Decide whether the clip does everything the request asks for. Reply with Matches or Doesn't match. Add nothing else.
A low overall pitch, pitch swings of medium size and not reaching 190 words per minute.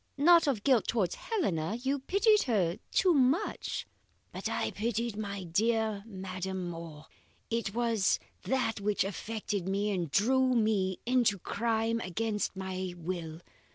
Doesn't match